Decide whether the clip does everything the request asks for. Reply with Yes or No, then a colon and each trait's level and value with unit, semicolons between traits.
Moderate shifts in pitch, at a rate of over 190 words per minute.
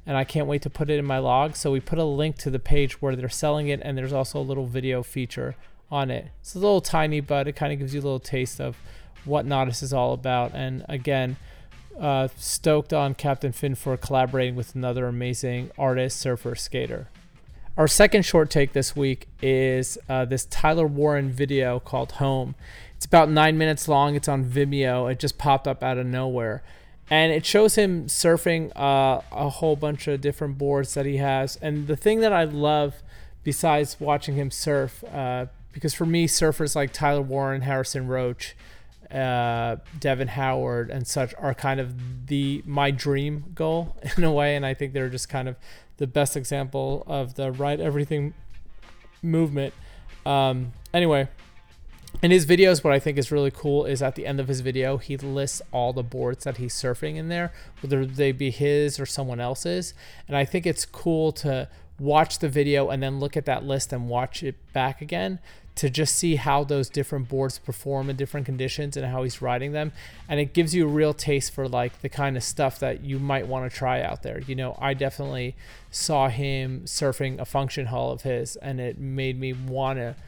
No: narrow, 2.1 semitones; average, 200 wpm